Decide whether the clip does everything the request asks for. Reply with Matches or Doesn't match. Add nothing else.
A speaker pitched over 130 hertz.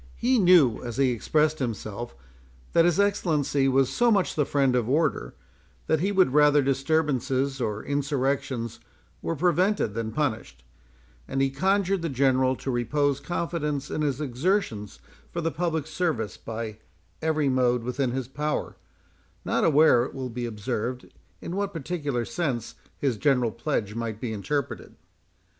Matches